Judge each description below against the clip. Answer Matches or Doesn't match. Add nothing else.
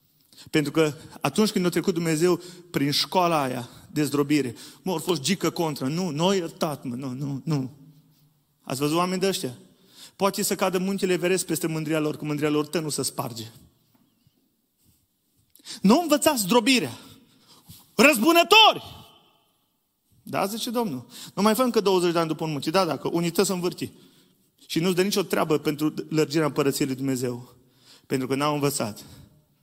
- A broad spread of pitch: Doesn't match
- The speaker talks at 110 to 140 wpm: Doesn't match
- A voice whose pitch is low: Doesn't match